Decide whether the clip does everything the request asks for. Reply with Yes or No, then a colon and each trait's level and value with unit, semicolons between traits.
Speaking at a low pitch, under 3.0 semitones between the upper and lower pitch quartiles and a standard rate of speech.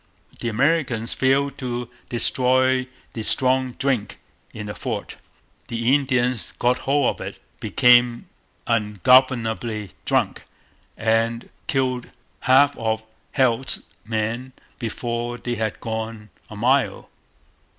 No: low, 120 Hz; narrow, 2.5 semitones; slow, 110 wpm